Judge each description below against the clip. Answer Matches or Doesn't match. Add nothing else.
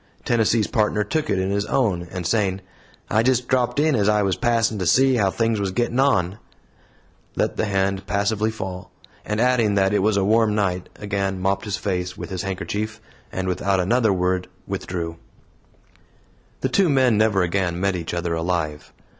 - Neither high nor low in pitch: Doesn't match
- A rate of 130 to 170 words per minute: Doesn't match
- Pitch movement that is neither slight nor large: Matches